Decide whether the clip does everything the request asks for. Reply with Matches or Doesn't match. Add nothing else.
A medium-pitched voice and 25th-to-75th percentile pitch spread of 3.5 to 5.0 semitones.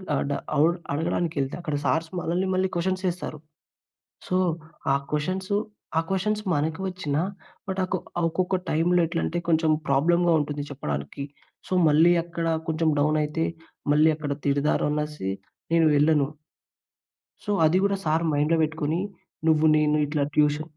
Doesn't match